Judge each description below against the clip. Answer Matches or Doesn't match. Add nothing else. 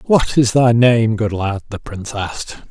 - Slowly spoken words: Doesn't match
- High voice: Doesn't match